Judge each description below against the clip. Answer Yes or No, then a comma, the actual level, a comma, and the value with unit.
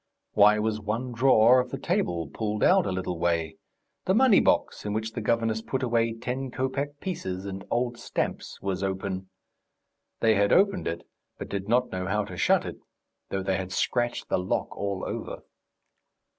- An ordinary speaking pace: Yes, average, 180 wpm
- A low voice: Yes, low, 105 Hz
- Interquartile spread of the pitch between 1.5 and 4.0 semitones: No, average, 4.4 semitones